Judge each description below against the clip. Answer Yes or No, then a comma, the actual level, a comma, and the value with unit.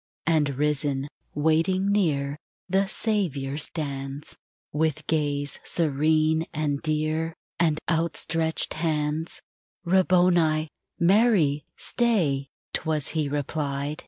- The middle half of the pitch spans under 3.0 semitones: Yes, narrow, 2.5 semitones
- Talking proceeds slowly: Yes, slow, 110 wpm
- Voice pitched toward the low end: No, medium, 155 Hz